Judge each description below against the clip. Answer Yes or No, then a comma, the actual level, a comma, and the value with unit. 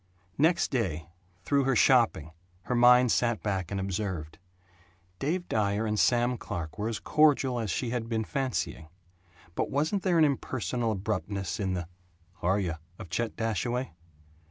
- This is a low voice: Yes, low, 115 Hz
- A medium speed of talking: Yes, average, 155 wpm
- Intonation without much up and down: No, average, 4.9 semitones